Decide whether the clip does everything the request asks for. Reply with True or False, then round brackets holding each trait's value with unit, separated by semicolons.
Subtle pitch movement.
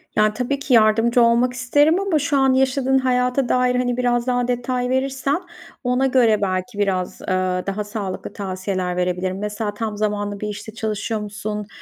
False (3.6 semitones)